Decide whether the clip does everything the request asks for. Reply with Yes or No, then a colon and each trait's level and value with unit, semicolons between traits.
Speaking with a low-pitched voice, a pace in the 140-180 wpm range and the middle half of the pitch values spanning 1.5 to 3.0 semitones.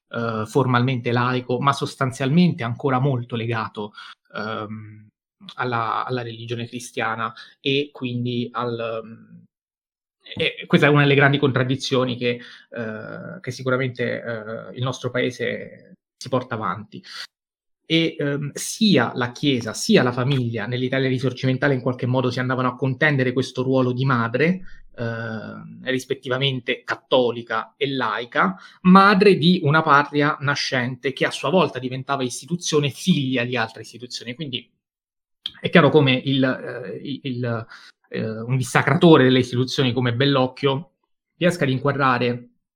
No: low, 130 Hz; average, 130 wpm; average, 2.7 semitones